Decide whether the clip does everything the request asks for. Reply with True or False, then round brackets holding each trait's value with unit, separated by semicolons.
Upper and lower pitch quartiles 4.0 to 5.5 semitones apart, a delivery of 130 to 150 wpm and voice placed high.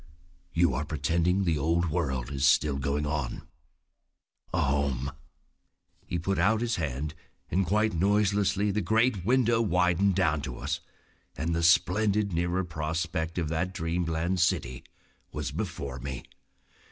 False (4.5 semitones; 140 wpm; 85 Hz)